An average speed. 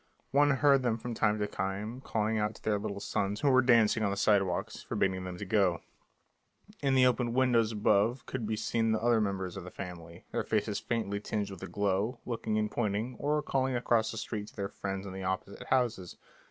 No: fast, 210 wpm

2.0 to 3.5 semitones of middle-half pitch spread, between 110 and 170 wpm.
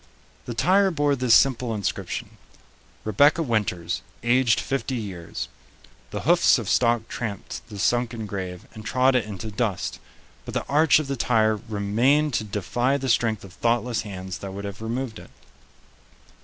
No: average, 4.0 semitones; average, 155 wpm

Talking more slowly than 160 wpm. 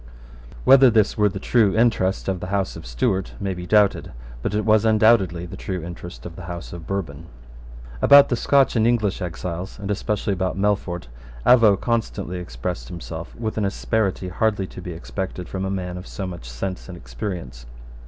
No: average, 190 wpm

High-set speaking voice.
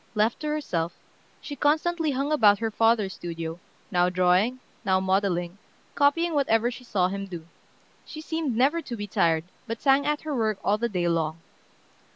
Yes: high, 220 Hz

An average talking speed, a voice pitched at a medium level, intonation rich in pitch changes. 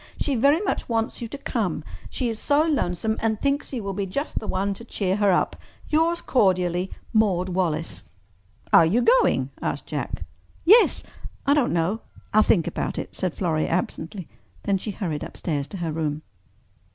No: average, 165 wpm; high, 200 Hz; wide, 5.7 semitones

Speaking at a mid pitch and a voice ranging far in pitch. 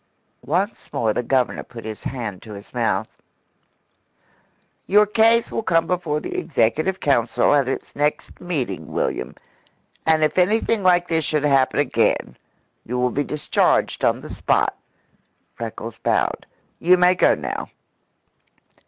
Yes: medium, 150 Hz; wide, 7.0 semitones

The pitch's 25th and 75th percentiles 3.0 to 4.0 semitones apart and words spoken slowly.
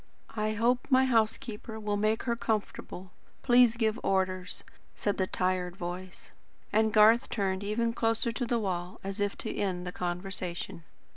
No: average, 3.5 semitones; average, 155 wpm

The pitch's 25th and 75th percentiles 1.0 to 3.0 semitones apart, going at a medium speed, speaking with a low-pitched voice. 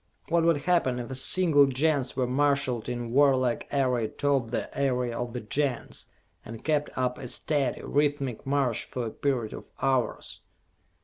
Yes: average, 2.7 semitones; average, 165 wpm; low, 130 Hz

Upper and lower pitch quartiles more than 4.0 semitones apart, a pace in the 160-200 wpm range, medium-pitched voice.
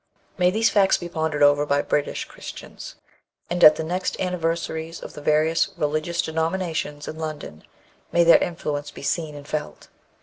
No: narrow, 2.5 semitones; average, 165 wpm; medium, 160 Hz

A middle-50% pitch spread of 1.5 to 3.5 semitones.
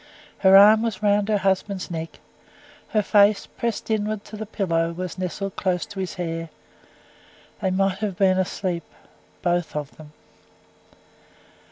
Yes: average, 2.8 semitones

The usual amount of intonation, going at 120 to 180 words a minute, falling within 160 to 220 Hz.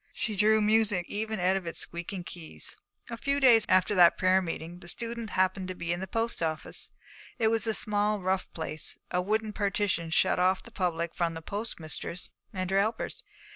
No: average, 3.8 semitones; average, 195 wpm; high, 190 Hz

